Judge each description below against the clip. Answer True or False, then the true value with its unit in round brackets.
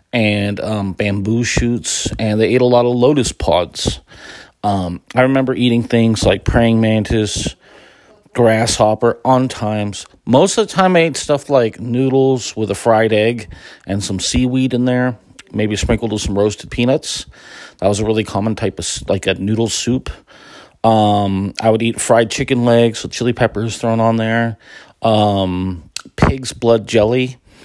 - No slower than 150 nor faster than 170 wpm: True (165 wpm)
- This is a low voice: True (110 Hz)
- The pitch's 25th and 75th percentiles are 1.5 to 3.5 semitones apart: True (2.8 semitones)